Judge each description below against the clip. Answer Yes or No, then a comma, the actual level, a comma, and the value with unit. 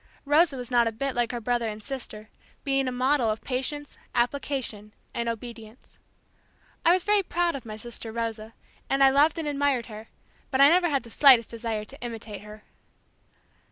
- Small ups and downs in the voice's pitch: No, average, 3.8 semitones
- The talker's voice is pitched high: Yes, high, 245 Hz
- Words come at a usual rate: Yes, average, 185 wpm